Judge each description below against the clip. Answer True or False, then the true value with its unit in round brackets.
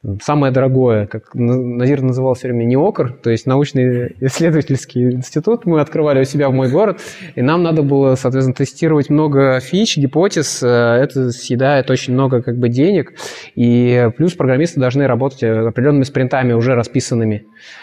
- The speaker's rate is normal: True (150 wpm)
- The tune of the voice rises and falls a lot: False (2.6 semitones)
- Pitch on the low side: True (130 Hz)